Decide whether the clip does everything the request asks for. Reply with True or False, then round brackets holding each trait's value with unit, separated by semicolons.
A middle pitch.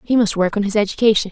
False (210 Hz)